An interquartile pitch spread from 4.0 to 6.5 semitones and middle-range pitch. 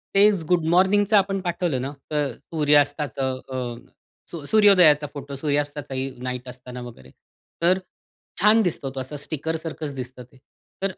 Yes: average, 5.2 semitones; medium, 145 Hz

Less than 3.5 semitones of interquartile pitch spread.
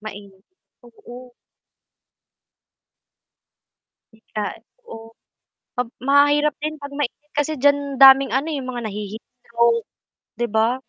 No: average, 4.0 semitones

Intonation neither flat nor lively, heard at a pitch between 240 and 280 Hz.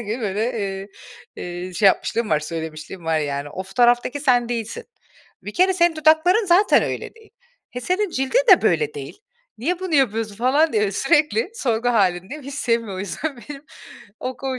No: wide, 7.7 semitones; high, 245 Hz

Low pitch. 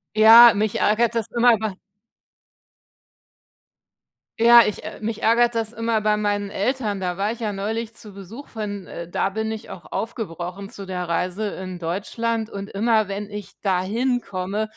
No: high, 210 Hz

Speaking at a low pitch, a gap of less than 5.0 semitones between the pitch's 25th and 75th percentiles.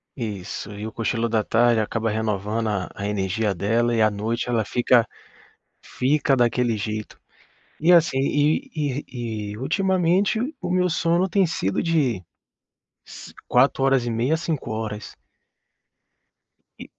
No: low, 115 Hz; wide, 5.6 semitones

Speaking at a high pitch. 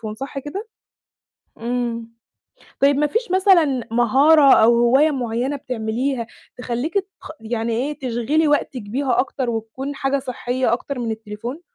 Yes: very high, 255 Hz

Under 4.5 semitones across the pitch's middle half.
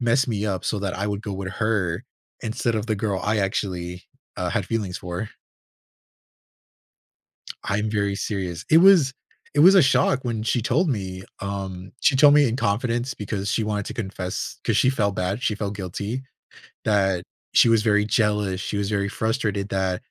Yes: average, 3.0 semitones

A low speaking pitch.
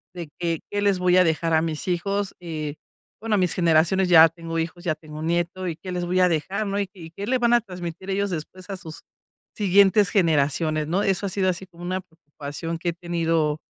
No: medium, 175 Hz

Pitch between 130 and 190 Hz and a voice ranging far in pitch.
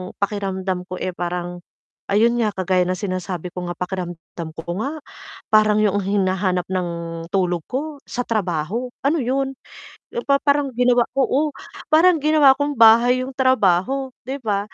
No: high, 210 Hz; wide, 6.4 semitones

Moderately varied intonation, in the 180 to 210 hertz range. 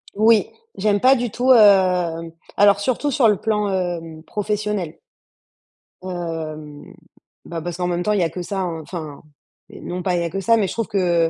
Yes: average, 3.9 semitones; medium, 185 Hz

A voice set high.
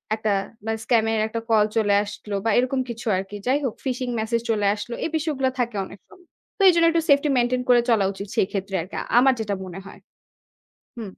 Yes: high, 230 Hz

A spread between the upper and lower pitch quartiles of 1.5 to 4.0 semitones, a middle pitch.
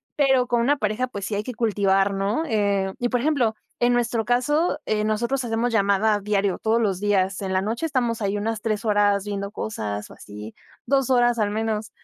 No: average, 3.2 semitones; high, 215 Hz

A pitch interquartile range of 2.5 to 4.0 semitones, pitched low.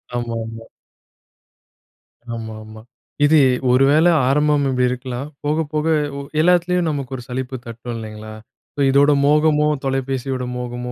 Yes: average, 3.6 semitones; low, 130 Hz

